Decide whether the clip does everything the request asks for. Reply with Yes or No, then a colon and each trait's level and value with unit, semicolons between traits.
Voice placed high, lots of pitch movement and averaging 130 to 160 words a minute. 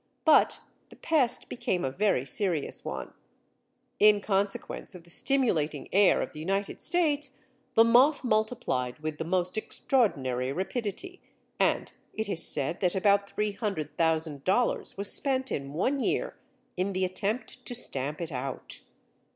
Yes: high, 195 Hz; wide, 7.0 semitones; average, 145 wpm